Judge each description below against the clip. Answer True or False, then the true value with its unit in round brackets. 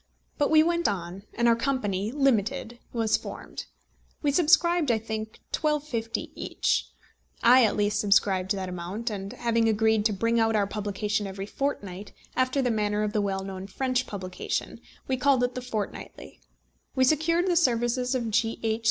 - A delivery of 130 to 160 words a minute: False (170 wpm)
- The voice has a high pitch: True (225 Hz)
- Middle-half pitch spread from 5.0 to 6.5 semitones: False (4.0 semitones)